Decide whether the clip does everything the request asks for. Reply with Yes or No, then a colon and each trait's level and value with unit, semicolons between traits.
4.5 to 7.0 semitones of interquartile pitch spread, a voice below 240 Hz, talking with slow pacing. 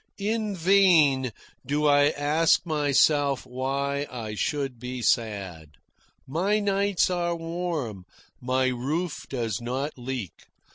Yes: average, 4.9 semitones; medium, 140 Hz; slow, 110 wpm